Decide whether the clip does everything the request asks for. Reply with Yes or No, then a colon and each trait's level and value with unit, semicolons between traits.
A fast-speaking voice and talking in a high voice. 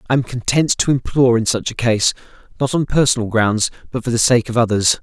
No: fast, 225 wpm; low, 120 Hz